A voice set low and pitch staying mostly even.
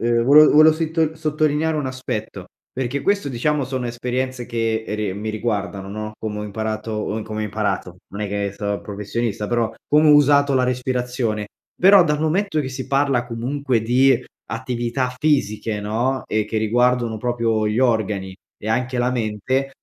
No: low, 120 Hz; average, 4.0 semitones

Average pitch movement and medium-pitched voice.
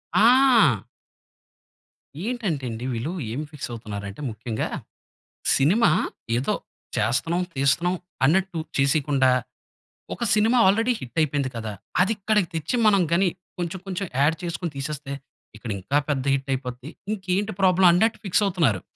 No: wide, 6.3 semitones; medium, 155 Hz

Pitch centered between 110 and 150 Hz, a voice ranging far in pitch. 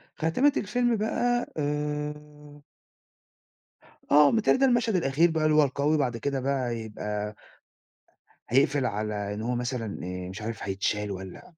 Yes: medium, 140 Hz; wide, 6.4 semitones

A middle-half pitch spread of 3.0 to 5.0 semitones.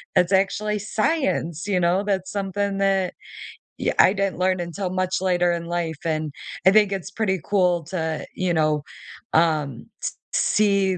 No: narrow, 2.5 semitones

